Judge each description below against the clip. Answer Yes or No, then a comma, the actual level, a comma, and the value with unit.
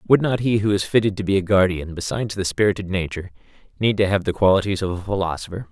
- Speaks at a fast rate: Yes, fast, 230 wpm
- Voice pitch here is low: Yes, low, 100 Hz